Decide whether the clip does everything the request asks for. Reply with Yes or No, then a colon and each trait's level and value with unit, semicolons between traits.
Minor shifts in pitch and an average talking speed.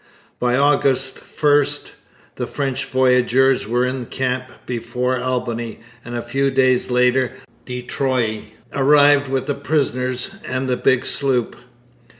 No: narrow, 1.4 semitones; slow, 130 wpm